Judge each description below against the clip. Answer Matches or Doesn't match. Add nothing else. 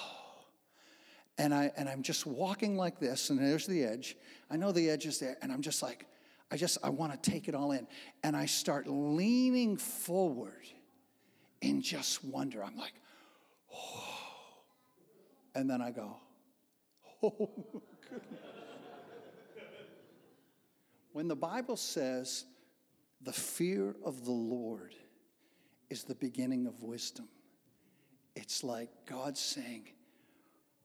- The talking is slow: Matches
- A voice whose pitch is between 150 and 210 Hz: Matches